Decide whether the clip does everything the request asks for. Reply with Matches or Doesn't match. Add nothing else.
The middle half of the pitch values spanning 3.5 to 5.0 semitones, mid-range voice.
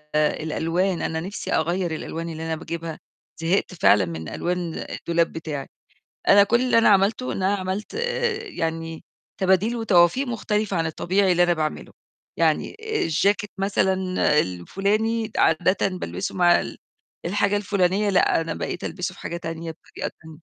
Matches